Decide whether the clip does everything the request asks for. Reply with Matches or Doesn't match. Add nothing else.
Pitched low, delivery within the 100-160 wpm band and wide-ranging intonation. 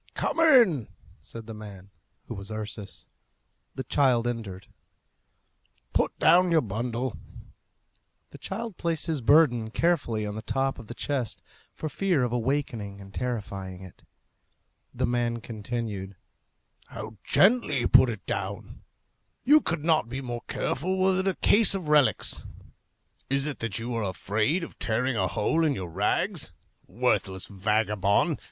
Matches